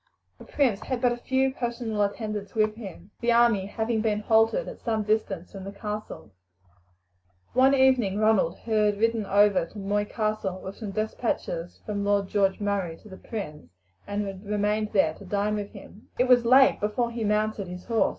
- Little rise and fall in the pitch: Yes, narrow, 2.3 semitones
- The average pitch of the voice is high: Yes, high, 210 Hz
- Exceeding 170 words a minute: Yes, average, 185 wpm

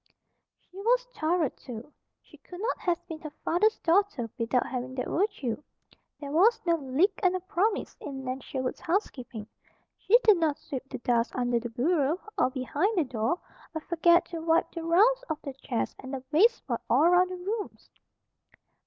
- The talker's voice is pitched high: Yes, very high, 320 Hz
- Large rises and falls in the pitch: Yes, wide, 6.0 semitones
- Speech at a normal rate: Yes, average, 180 wpm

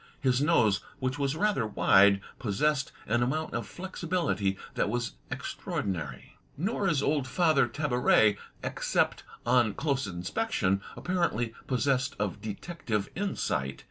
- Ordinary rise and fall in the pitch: No, wide, 7.0 semitones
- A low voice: Yes, low, 125 Hz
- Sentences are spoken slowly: Yes, slow, 120 wpm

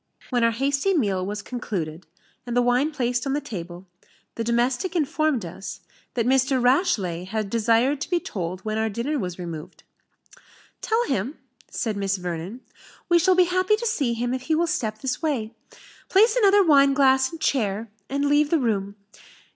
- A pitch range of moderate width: No, wide, 6.2 semitones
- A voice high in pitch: Yes, high, 245 Hz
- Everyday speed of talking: Yes, average, 175 wpm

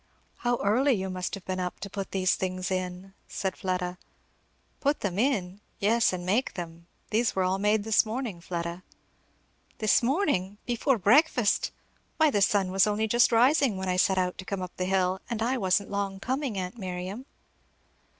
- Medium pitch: No, high, 195 Hz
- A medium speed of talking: Yes, average, 180 wpm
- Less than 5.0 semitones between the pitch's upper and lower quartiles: Yes, average, 4.0 semitones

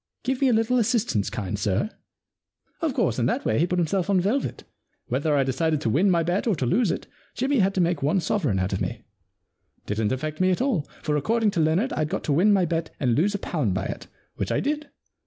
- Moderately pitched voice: Yes, medium, 170 Hz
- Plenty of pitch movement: Yes, wide, 7.1 semitones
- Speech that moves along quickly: Yes, fast, 250 wpm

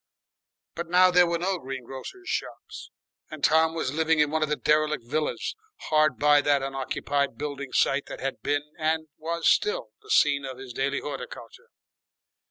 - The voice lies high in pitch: No, medium, 150 Hz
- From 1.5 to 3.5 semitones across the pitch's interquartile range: Yes, average, 2.7 semitones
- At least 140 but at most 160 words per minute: No, average, 175 wpm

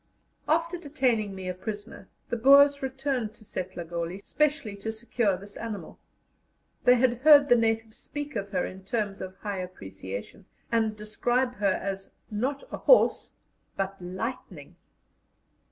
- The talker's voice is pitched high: Yes, high, 220 Hz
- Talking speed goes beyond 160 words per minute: No, average, 140 wpm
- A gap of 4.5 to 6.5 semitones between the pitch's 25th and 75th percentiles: Yes, average, 5.0 semitones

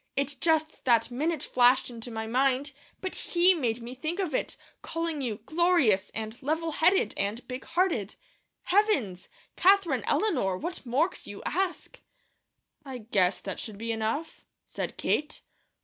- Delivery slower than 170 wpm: Yes, average, 150 wpm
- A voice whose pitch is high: Yes, very high, 265 Hz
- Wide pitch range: Yes, wide, 6.7 semitones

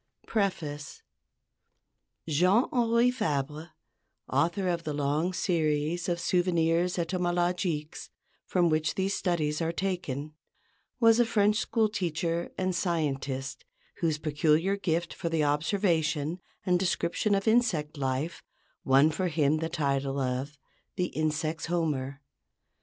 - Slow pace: Yes, slow, 120 wpm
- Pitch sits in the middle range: Yes, medium, 165 Hz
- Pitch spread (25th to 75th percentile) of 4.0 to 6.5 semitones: No, average, 3.4 semitones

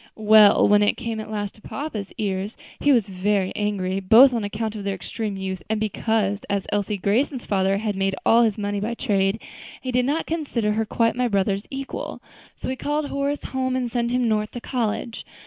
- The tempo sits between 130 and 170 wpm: No, fast, 205 wpm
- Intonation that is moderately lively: Yes, average, 3.3 semitones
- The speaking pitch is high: Yes, high, 215 Hz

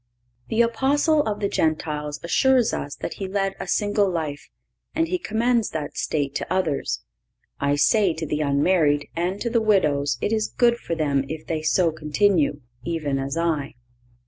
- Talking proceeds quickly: No, average, 170 wpm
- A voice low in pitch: No, medium, 170 Hz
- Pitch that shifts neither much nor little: No, wide, 6.3 semitones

